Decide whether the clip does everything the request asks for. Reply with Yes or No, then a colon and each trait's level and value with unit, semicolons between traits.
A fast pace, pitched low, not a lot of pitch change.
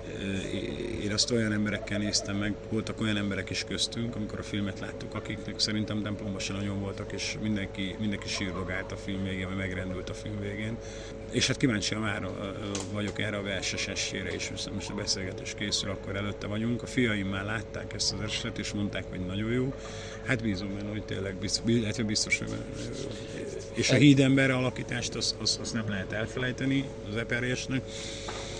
Yes: fast, 175 wpm; low, 110 Hz; narrow, 1.7 semitones